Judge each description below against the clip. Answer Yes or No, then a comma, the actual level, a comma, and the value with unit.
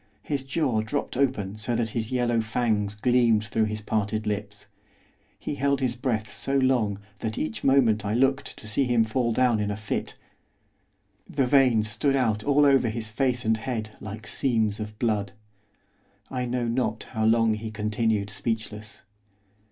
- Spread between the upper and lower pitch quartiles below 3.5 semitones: Yes, average, 2.9 semitones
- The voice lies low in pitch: Yes, low, 115 Hz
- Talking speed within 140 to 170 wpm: Yes, average, 165 wpm